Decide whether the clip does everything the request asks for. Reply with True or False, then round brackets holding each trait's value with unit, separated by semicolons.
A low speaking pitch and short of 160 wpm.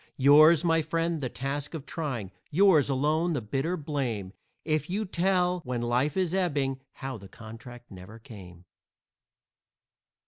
False (145 Hz; 140 wpm)